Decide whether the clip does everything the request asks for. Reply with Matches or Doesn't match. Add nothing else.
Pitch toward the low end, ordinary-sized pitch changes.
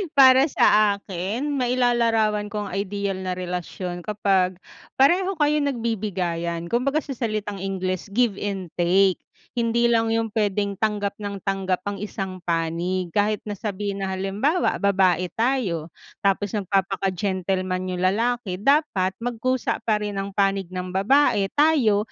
Doesn't match